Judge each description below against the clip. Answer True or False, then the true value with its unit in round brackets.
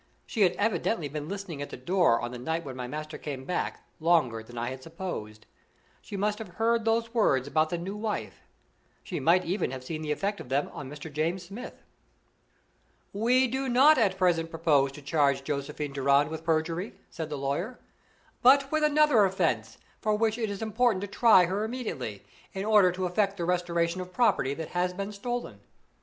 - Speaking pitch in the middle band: True (175 Hz)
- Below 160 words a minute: False (195 wpm)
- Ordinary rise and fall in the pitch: False (6.3 semitones)